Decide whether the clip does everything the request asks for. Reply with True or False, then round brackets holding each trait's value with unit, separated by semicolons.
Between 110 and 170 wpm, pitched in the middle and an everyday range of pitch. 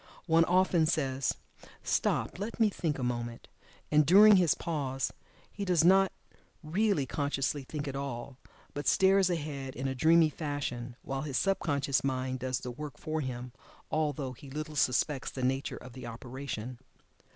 True (160 wpm; 145 Hz; 3.9 semitones)